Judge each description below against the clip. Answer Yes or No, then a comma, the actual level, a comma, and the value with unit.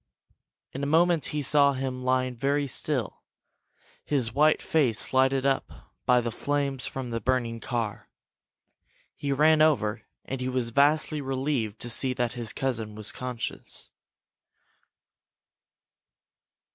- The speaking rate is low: Yes, slow, 130 wpm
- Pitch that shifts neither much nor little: Yes, average, 3.0 semitones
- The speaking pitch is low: Yes, low, 130 Hz